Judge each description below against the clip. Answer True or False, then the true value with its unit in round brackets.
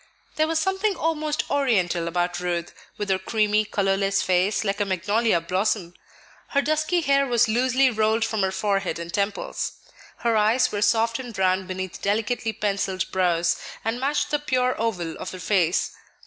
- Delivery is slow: False (165 wpm)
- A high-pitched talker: True (210 Hz)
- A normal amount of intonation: True (5.0 semitones)